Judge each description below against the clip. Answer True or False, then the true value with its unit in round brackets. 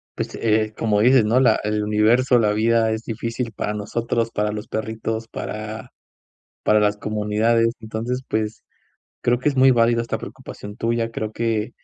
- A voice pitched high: False (110 Hz)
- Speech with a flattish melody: True (1.5 semitones)